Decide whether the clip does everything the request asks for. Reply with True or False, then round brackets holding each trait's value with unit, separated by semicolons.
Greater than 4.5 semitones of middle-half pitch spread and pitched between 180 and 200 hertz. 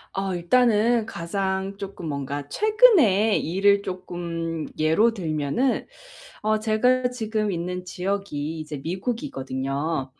True (5.1 semitones; 190 Hz)